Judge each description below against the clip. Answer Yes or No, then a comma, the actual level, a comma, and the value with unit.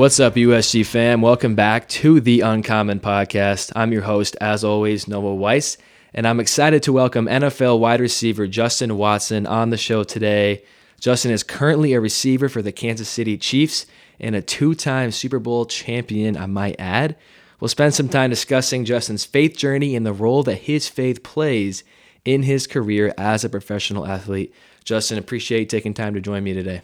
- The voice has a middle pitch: No, low, 115 Hz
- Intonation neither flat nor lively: Yes, average, 3.8 semitones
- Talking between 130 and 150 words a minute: No, average, 185 wpm